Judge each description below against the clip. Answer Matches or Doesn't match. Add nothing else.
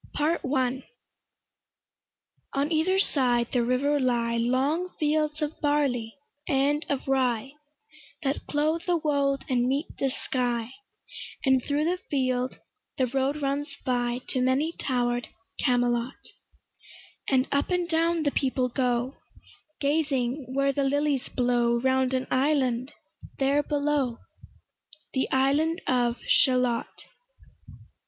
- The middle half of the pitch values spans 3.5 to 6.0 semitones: Doesn't match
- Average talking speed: Doesn't match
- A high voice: Matches